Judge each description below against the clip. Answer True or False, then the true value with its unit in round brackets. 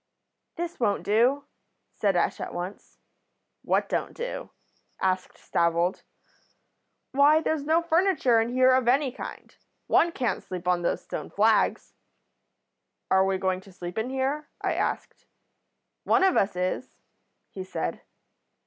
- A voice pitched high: True (230 Hz)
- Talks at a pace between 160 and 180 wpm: False (140 wpm)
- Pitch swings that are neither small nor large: False (7.5 semitones)